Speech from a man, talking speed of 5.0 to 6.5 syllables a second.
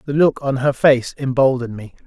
Yes: male; 5.6 syllables/s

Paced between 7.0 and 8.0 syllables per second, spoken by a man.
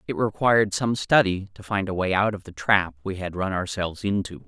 No: 5.5 syllables/s; male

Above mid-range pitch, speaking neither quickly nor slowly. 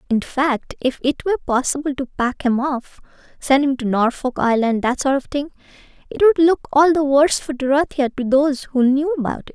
Yes: very high, 275 Hz; average, 190 wpm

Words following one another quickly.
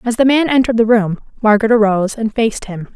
Yes: fast, 225 wpm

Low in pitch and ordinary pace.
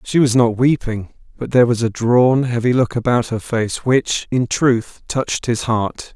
Yes: low, 120 Hz; average, 195 wpm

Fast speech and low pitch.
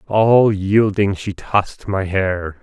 No: slow, 135 wpm; low, 100 Hz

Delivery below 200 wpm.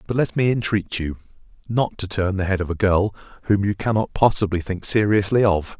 No: fast, 205 wpm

